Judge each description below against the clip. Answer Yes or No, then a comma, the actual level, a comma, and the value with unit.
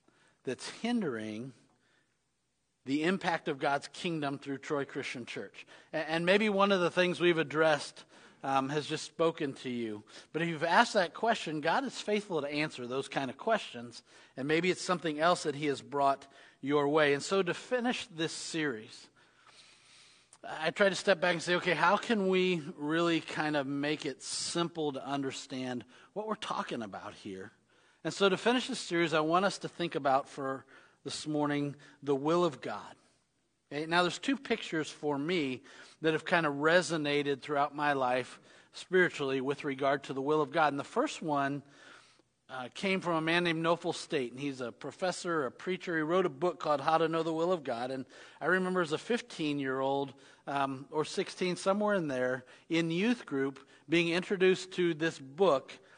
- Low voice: No, medium, 155 Hz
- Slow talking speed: No, average, 190 wpm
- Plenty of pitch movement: No, average, 4.3 semitones